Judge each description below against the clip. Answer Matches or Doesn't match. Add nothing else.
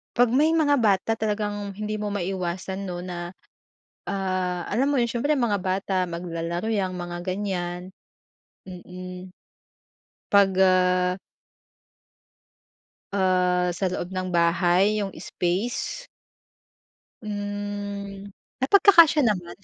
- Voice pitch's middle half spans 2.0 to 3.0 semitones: Matches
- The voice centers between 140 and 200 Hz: Matches